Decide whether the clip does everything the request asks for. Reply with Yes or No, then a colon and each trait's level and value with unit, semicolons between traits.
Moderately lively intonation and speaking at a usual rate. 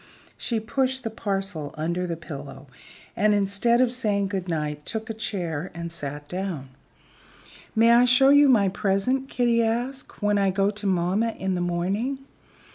Yes: average, 4.8 semitones; average, 160 wpm